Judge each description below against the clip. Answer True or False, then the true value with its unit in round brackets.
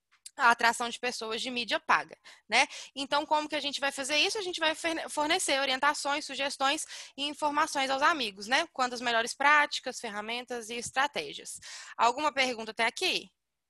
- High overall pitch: True (275 Hz)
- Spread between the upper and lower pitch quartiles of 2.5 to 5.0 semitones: True (3.7 semitones)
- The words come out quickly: False (165 wpm)